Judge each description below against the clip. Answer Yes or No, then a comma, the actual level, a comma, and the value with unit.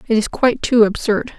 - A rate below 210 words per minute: No, fast, 215 wpm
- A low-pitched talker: No, high, 230 Hz